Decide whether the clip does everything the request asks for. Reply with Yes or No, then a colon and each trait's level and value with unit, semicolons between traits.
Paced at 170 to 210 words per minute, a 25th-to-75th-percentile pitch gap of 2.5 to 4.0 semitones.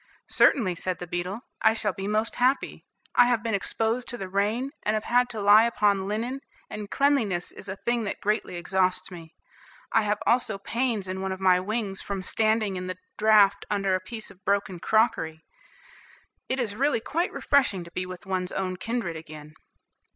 Yes: average, 190 wpm; average, 3.4 semitones